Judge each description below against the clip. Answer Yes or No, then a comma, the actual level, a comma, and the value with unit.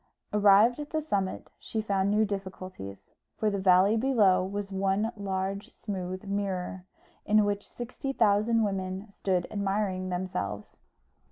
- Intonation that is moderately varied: No, narrow, 2.1 semitones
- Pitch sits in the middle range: No, high, 200 Hz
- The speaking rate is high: No, slow, 135 wpm